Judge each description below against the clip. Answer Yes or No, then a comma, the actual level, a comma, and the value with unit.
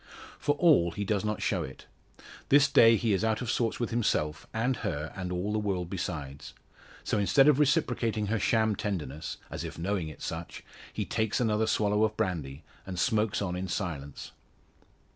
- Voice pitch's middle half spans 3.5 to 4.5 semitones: Yes, average, 4.2 semitones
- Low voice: Yes, low, 105 Hz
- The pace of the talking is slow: No, average, 180 wpm